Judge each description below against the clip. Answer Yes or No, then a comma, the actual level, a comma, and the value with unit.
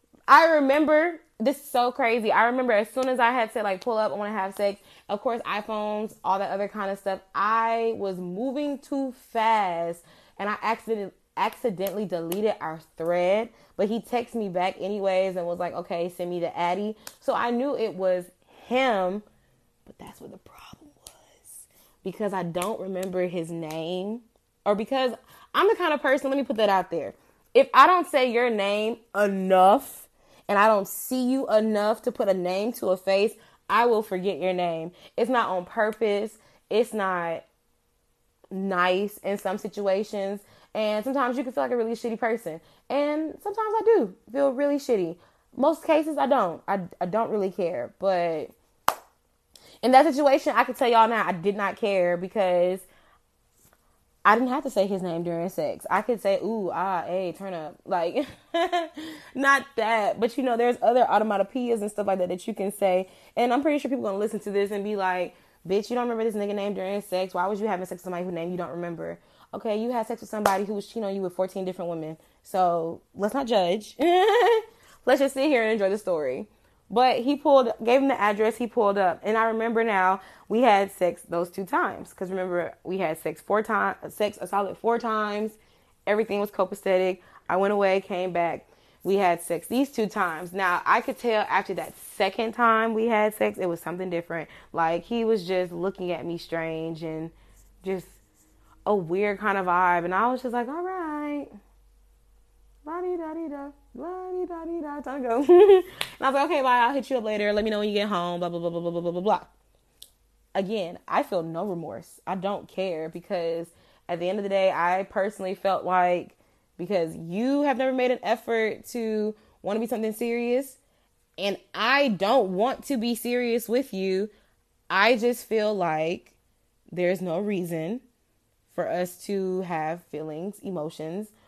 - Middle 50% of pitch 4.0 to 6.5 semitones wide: Yes, average, 4.8 semitones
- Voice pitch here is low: No, high, 205 Hz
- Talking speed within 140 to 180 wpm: No, average, 195 wpm